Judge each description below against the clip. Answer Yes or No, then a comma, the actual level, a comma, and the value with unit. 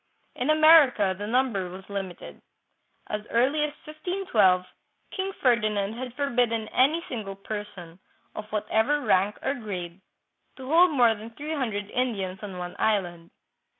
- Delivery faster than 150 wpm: No, average, 145 wpm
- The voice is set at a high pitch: Yes, high, 220 Hz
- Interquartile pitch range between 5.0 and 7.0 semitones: Yes, wide, 5.5 semitones